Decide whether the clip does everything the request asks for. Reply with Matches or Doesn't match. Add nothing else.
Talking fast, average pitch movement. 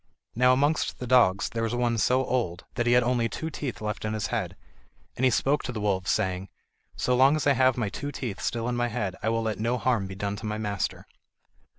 Matches